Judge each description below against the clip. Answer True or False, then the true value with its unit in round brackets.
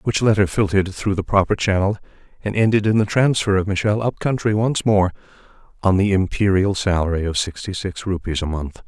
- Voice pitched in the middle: False (100 Hz)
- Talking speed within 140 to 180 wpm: False (190 wpm)